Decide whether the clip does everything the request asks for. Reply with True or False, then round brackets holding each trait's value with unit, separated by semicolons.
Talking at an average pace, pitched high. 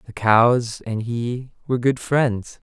False (155 wpm; 120 Hz)